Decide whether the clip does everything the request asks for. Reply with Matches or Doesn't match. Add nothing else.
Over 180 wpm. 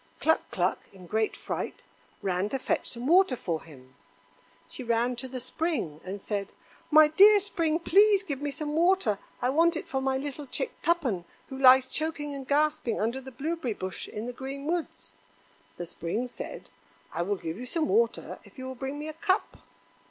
Matches